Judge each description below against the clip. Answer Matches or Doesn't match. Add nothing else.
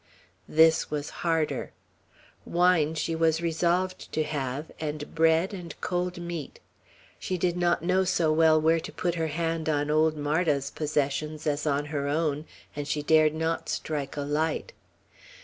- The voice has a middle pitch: Matches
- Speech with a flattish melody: Matches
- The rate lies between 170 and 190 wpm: Doesn't match